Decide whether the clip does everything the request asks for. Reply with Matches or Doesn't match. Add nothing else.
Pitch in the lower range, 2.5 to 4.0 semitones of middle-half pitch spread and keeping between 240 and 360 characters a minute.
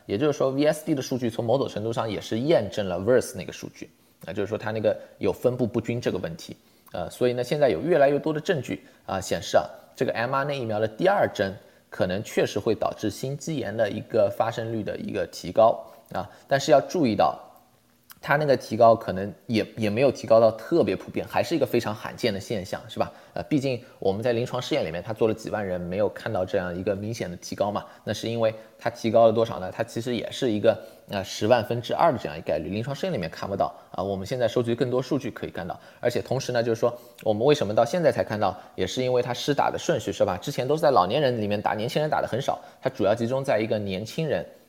Doesn't match